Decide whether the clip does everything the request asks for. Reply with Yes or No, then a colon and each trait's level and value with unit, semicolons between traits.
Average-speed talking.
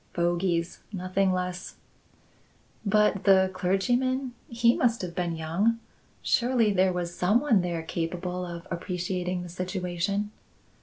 No: slow, 120 wpm